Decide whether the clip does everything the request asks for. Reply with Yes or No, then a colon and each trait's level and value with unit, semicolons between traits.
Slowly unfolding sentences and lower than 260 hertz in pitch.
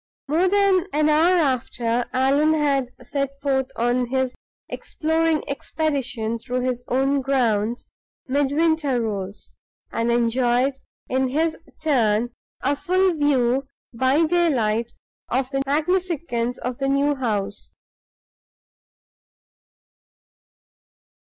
No: slow, 100 wpm; very high, 270 Hz